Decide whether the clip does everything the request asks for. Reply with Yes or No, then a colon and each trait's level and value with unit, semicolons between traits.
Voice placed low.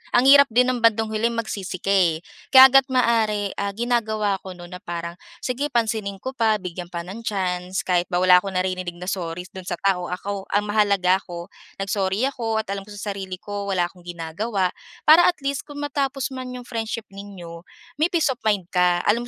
No: high, 200 Hz